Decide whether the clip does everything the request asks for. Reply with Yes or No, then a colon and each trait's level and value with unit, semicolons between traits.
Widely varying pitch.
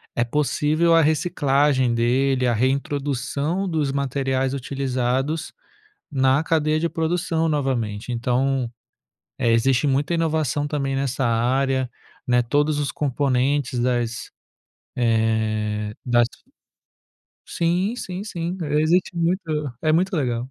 No: average, 4.0 semitones